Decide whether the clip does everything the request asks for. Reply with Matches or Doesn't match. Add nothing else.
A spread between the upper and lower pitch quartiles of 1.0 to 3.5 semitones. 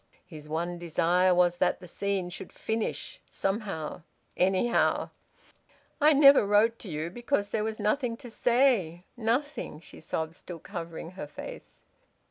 Doesn't match